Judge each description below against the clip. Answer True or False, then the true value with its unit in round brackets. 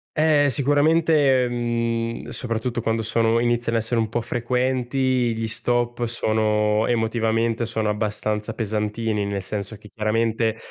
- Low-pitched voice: True (115 Hz)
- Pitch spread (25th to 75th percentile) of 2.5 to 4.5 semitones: False (1.8 semitones)